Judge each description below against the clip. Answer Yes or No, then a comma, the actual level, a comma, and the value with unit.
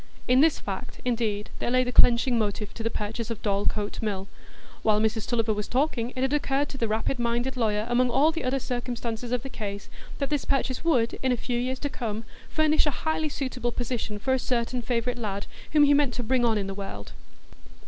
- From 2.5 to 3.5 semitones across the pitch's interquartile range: Yes, average, 3.2 semitones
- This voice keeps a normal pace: No, fast, 220 wpm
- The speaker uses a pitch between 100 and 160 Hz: No, high, 240 Hz